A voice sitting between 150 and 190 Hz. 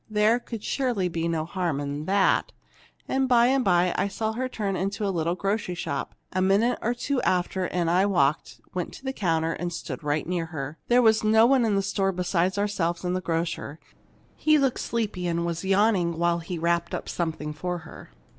Yes: medium, 185 Hz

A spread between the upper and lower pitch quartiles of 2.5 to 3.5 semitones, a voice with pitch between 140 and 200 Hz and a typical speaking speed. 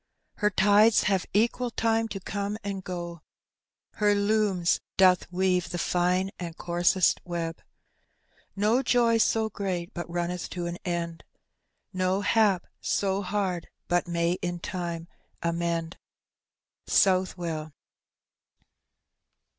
No: average, 2.8 semitones; medium, 185 Hz; slow, 115 wpm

